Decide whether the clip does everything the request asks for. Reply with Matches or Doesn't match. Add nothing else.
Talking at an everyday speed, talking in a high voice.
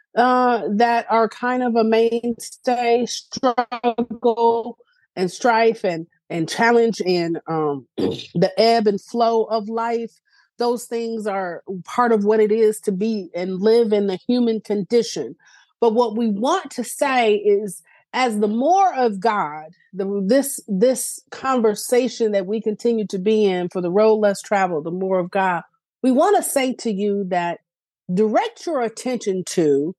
Matches